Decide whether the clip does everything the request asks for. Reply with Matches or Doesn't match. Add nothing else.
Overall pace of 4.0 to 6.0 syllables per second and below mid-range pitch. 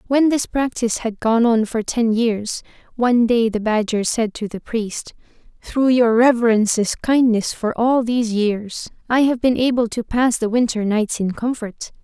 Doesn't match